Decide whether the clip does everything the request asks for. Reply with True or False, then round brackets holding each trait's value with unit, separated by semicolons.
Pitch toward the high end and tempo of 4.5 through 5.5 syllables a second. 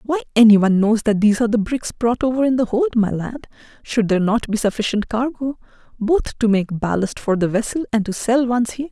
False (230 Hz; 5.8 syllables/s)